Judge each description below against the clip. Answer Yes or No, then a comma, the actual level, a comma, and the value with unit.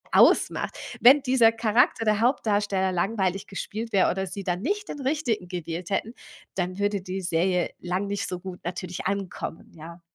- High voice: Yes, high, 195 Hz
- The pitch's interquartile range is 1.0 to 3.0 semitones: No, average, 3.8 semitones